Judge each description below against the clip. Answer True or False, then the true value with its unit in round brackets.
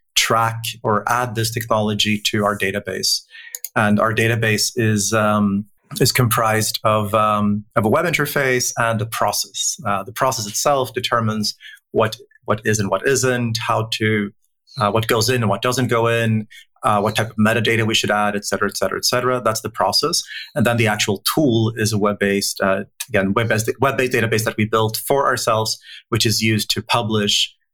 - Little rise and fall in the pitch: True (2.2 semitones)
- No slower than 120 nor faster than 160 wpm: False (195 wpm)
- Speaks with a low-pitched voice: True (110 Hz)